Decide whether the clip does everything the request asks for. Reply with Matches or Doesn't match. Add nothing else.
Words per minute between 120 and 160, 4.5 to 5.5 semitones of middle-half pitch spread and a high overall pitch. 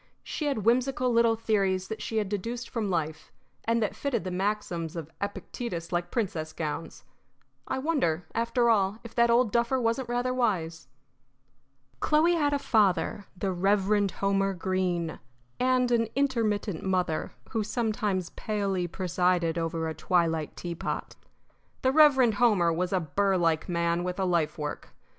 Matches